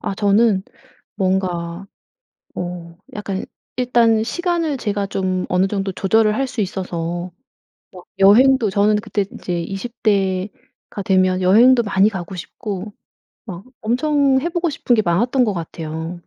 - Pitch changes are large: No, average, 4.1 semitones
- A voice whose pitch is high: Yes, high, 200 Hz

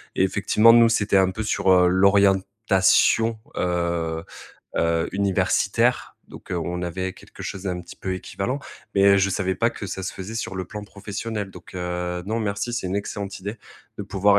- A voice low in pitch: Yes, very low, 95 Hz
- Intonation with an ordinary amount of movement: No, narrow, 2.1 semitones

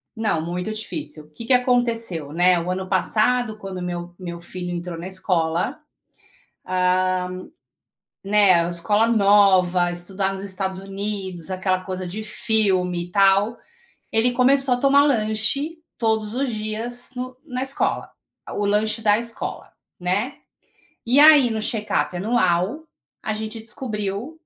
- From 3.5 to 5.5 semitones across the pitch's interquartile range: Yes, average, 4.1 semitones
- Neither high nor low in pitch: No, high, 205 Hz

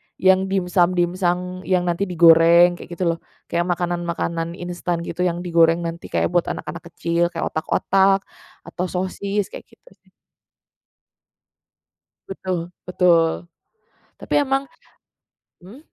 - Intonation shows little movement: Yes, narrow, 1.5 semitones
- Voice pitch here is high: No, medium, 175 Hz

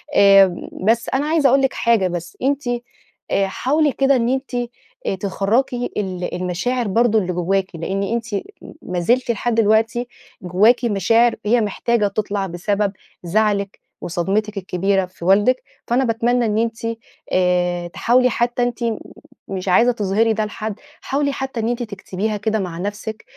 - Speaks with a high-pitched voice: Yes, high, 215 Hz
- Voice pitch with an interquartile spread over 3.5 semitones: Yes, average, 3.9 semitones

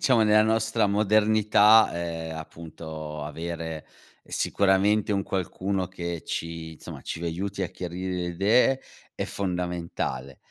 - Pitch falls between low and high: No, very low, 90 Hz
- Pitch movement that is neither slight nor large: Yes, average, 3.9 semitones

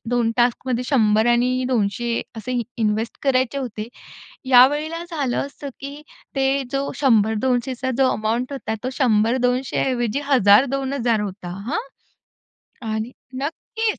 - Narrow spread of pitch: No, average, 3.3 semitones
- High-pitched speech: Yes, very high, 250 Hz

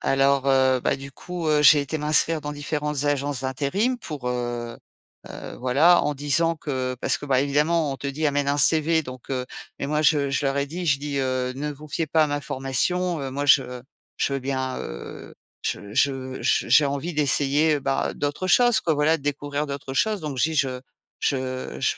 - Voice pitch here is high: No, medium, 140 Hz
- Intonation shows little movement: Yes, narrow, 2.3 semitones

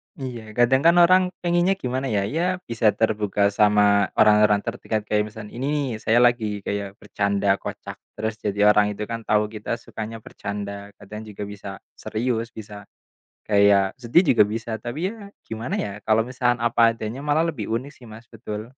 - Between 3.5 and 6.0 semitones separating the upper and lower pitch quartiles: No, average, 2.7 semitones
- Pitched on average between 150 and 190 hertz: No, low, 110 Hz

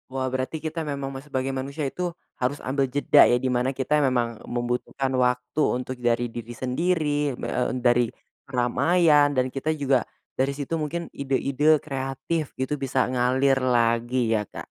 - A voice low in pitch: Yes, low, 130 Hz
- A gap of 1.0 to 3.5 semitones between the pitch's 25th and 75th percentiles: Yes, narrow, 2.6 semitones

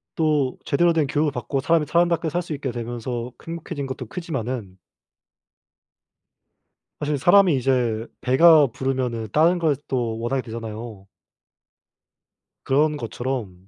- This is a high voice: No, low, 135 Hz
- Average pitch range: Yes, average, 4.8 semitones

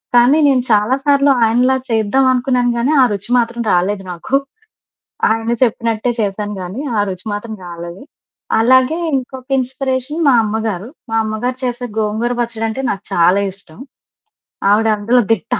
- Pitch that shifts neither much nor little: Yes, average, 3.6 semitones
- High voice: Yes, high, 230 Hz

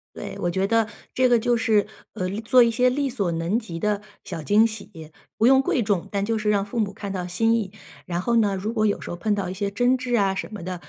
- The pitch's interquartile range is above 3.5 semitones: No, average, 3.2 semitones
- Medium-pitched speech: No, high, 210 Hz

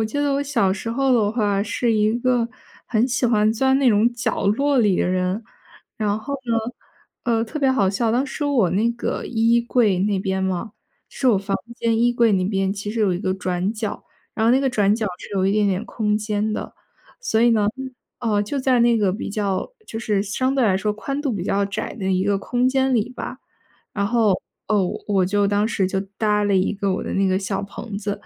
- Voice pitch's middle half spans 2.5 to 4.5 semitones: Yes, average, 3.2 semitones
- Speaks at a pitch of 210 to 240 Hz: Yes, high, 215 Hz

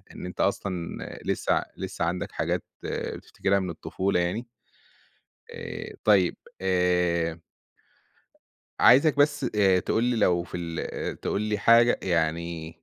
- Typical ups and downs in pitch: Yes, average, 3.7 semitones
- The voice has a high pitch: No, very low, 90 Hz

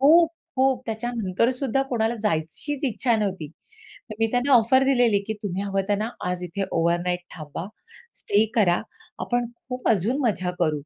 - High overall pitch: Yes, high, 220 Hz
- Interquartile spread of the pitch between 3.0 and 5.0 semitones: No, wide, 5.5 semitones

